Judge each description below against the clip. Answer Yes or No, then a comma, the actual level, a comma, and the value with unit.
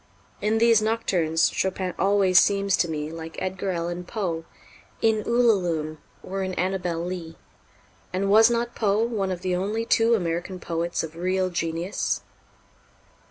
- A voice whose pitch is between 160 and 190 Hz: Yes, medium, 185 Hz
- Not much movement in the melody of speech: No, average, 3.5 semitones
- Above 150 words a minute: No, average, 145 wpm